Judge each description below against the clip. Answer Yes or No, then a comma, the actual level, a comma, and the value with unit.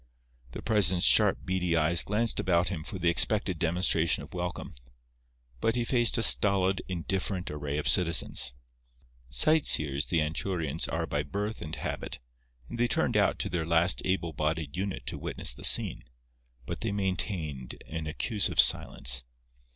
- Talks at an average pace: Yes, average, 160 wpm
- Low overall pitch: Yes, very low, 85 Hz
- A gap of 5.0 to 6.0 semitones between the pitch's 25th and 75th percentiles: No, average, 3.8 semitones